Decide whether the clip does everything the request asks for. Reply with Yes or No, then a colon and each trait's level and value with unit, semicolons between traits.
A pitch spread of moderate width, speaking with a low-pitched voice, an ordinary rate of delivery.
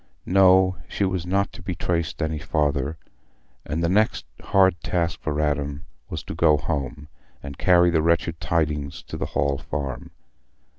Yes: average, 3.4 semitones; very low, 80 Hz; average, 160 wpm